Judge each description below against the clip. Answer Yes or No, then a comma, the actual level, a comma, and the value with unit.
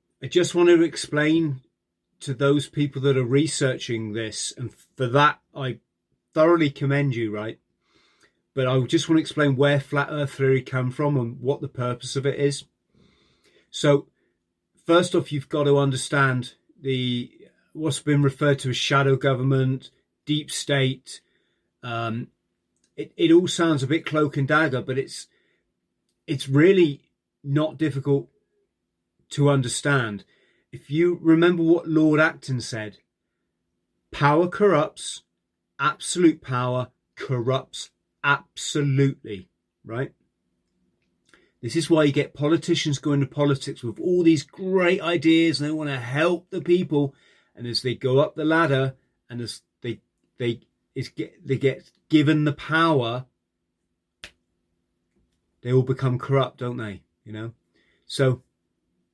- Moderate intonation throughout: Yes, average, 4.5 semitones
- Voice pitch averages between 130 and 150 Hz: Yes, low, 135 Hz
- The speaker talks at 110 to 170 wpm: Yes, average, 140 wpm